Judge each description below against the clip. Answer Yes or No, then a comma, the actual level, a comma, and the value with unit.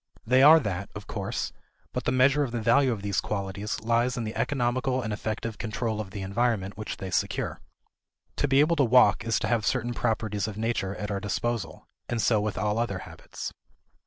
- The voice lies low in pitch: Yes, low, 110 Hz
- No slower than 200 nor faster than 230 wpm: Yes, fast, 205 wpm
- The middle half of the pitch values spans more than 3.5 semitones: No, average, 3.0 semitones